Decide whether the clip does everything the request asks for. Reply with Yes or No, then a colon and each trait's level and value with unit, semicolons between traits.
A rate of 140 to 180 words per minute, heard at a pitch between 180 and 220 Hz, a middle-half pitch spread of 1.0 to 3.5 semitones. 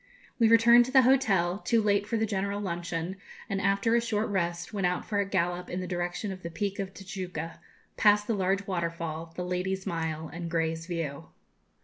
No: average, 200 wpm; high, 190 Hz; average, 3.2 semitones